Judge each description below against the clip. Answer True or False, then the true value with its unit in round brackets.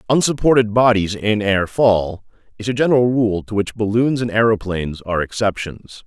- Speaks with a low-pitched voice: True (110 Hz)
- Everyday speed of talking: True (160 wpm)